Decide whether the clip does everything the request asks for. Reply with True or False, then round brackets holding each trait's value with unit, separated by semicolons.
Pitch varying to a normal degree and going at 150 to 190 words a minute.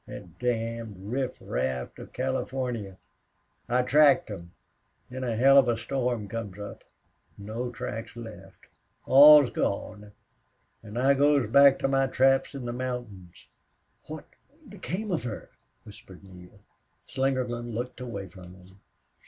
False (4.6 semitones; 135 wpm)